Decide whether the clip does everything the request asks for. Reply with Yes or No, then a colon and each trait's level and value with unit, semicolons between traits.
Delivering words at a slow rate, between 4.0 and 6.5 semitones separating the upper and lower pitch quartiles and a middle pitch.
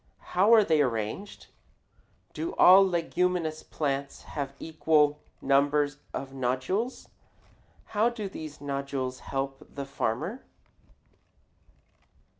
Yes: slow, 95 wpm; average, 4.9 semitones; medium, 150 Hz